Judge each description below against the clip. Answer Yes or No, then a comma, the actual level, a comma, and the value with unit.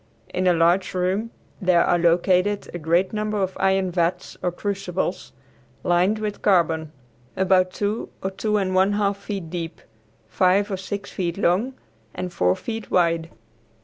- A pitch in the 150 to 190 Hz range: Yes, medium, 185 Hz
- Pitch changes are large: No, narrow, 2.4 semitones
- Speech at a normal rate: Yes, average, 155 wpm